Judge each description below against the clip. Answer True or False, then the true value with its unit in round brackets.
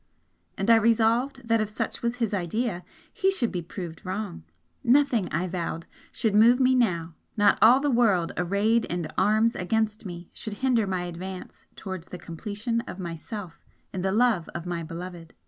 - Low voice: False (205 Hz)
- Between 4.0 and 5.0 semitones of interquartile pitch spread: True (4.6 semitones)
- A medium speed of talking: True (175 wpm)